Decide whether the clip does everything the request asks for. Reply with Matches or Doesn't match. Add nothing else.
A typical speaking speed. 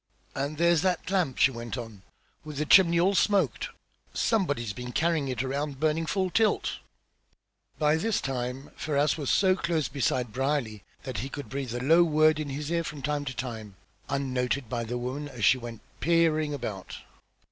Matches